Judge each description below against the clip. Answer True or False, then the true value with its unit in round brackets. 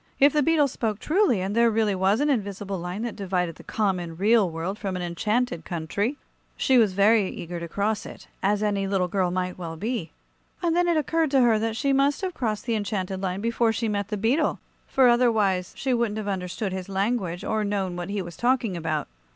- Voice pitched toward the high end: True (205 Hz)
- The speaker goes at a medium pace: False (215 wpm)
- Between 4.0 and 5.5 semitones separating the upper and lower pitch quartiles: True (4.3 semitones)